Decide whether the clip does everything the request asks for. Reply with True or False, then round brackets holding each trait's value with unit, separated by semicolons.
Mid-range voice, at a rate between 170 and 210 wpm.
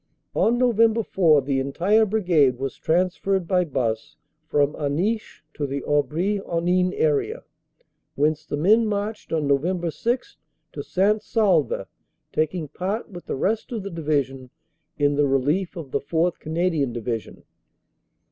False (165 Hz; 145 wpm)